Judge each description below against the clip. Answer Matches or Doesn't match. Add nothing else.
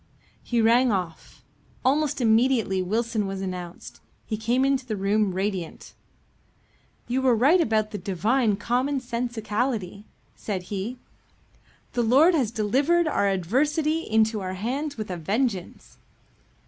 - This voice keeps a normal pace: Doesn't match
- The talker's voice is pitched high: Matches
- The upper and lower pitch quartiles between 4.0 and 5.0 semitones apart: Matches